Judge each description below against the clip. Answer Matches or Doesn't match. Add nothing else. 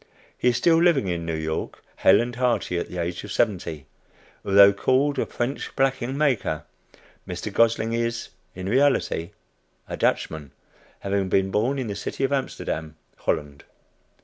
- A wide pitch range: Matches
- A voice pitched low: Matches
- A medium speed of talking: Matches